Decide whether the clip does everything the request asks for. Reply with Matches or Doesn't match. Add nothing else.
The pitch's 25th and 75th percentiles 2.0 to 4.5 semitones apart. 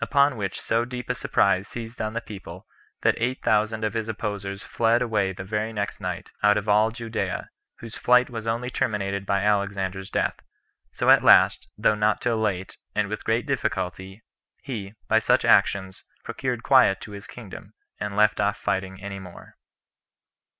Matches